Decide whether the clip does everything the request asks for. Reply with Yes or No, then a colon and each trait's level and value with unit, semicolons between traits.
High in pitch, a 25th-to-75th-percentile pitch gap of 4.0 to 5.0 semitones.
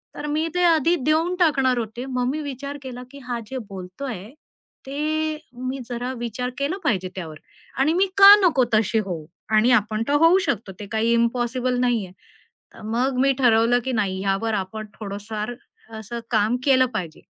Yes: high, 245 Hz; average, 4.5 semitones